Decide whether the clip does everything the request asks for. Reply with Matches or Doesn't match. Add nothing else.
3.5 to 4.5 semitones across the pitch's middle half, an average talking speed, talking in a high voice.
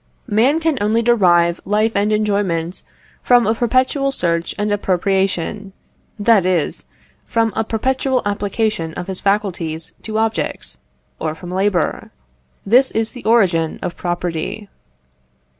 Doesn't match